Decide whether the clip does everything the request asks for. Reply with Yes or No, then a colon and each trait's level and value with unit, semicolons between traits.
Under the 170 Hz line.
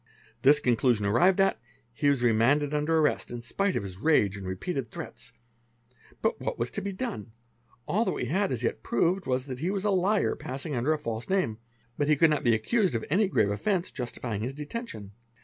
Yes: medium, 140 Hz